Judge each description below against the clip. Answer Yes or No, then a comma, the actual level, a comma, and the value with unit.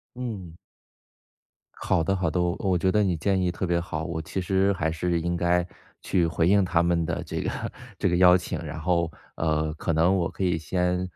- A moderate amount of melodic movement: No, narrow, 2.0 semitones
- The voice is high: No, very low, 90 Hz